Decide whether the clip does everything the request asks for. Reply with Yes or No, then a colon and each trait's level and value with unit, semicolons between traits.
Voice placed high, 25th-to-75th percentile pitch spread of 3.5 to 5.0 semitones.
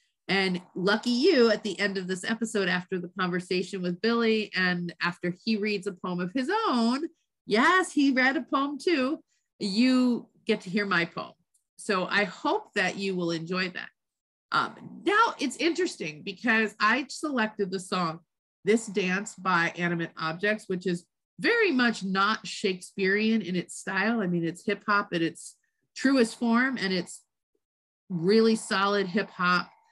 Yes: high, 205 Hz; average, 4.5 semitones